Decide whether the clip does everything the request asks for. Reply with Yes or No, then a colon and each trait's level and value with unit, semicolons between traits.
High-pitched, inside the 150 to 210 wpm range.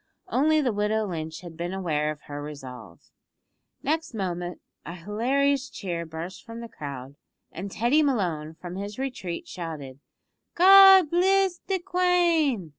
No: high, 200 Hz; average, 140 wpm